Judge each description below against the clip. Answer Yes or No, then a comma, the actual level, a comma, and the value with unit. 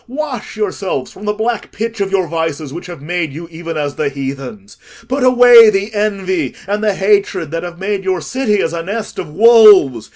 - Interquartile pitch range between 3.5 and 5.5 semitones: Yes, average, 4.7 semitones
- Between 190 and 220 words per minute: Yes, average, 195 wpm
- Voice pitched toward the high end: Yes, high, 195 Hz